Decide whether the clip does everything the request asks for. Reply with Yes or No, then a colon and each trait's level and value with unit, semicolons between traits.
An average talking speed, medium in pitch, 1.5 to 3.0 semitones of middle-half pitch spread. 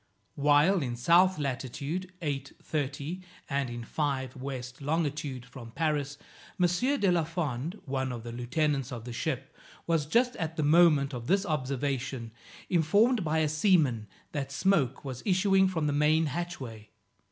No: average, 150 wpm; medium, 145 Hz; average, 4.2 semitones